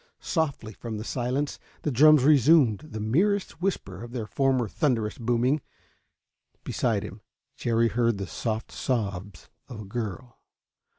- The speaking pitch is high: No, low, 120 Hz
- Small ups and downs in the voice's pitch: No, average, 4.4 semitones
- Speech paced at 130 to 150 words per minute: Yes, slow, 135 wpm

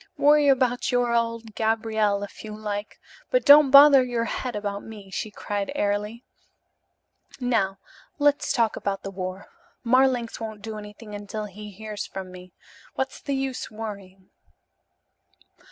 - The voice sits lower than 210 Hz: No, high, 220 Hz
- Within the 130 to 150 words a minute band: Yes, average, 140 wpm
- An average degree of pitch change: Yes, average, 3.4 semitones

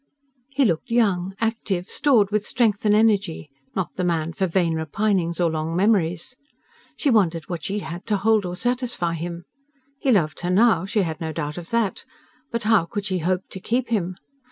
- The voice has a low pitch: No, high, 190 Hz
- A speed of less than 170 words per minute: No, average, 190 wpm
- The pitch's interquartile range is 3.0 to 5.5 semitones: Yes, average, 4.5 semitones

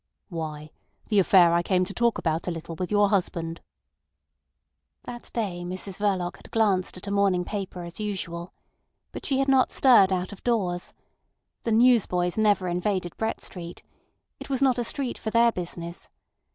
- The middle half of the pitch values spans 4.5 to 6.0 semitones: No, average, 4.0 semitones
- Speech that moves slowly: No, average, 170 wpm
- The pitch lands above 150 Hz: Yes, high, 190 Hz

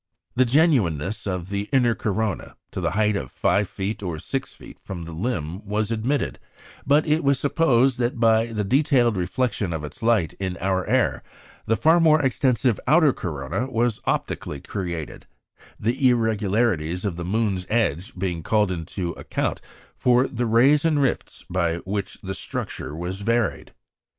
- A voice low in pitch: Yes, low, 110 Hz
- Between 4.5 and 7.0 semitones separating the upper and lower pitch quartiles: Yes, average, 5.2 semitones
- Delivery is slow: No, average, 160 wpm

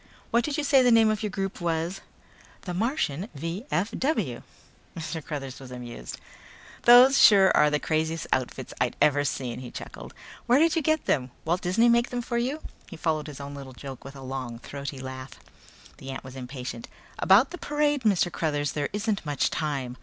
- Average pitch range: No, wide, 9.0 semitones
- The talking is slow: No, average, 185 wpm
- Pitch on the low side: No, medium, 160 Hz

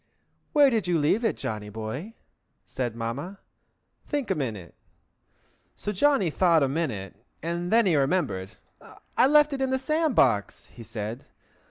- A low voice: No, medium, 165 Hz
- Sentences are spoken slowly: No, average, 155 wpm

